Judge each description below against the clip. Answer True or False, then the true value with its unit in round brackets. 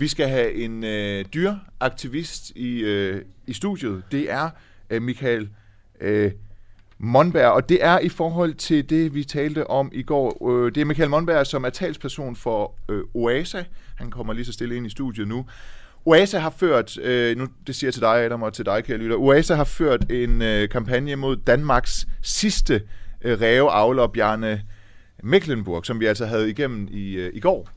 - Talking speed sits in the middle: True (185 wpm)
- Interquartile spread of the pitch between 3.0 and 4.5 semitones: False (5.2 semitones)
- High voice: False (120 Hz)